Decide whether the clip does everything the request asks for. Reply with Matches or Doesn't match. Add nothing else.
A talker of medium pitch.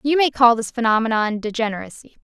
Doesn't match